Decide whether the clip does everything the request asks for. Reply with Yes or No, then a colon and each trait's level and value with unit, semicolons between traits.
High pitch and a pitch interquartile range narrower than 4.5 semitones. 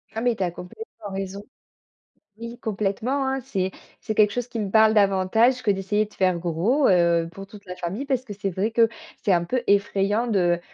Yes: high, 205 Hz; average, 3.5 semitones